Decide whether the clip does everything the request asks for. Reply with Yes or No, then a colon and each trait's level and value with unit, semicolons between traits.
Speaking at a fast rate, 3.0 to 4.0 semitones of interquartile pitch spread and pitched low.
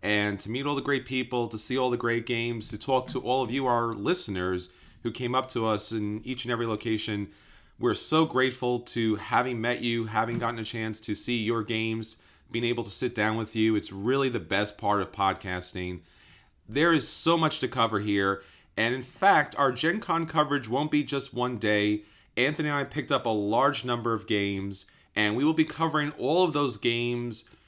Yes: fast, 210 wpm; average, 3.7 semitones; low, 115 Hz